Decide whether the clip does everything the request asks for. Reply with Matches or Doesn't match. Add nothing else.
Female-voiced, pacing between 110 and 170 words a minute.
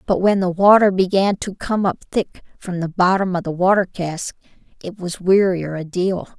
Doesn't match